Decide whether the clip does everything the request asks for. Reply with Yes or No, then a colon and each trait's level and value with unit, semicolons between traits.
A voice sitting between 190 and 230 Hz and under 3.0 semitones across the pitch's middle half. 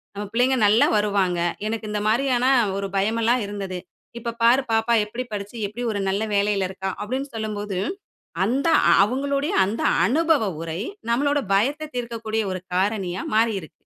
No: high, 220 Hz; average, 3.6 semitones